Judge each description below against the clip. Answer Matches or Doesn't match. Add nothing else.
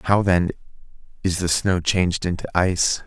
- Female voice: Doesn't match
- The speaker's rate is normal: Matches